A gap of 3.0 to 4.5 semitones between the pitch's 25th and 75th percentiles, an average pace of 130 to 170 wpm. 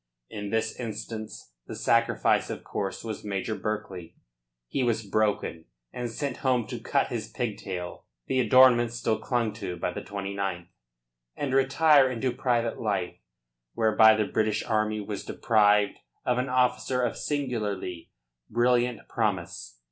Yes: average, 3.3 semitones; average, 140 wpm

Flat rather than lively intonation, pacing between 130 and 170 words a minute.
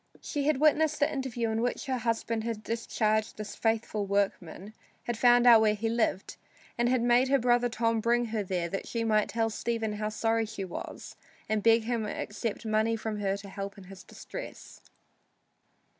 No: narrow, 2.1 semitones; average, 195 wpm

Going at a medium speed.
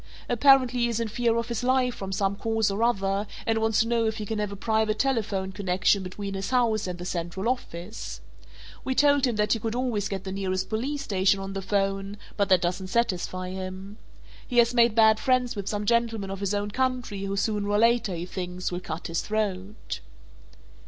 No: fast, 215 wpm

